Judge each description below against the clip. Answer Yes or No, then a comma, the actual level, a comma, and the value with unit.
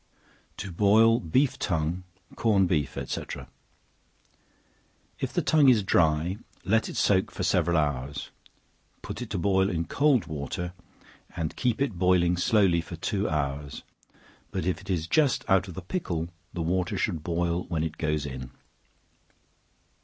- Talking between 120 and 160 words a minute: Yes, average, 150 wpm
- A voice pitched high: No, very low, 90 Hz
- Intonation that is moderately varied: Yes, average, 3.8 semitones